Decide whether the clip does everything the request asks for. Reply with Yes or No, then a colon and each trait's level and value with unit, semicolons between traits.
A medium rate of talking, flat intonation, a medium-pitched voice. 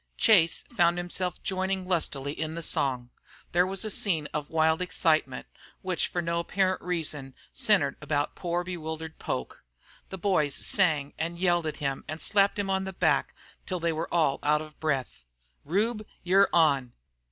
No: average, 165 wpm; average, 3.5 semitones; medium, 170 Hz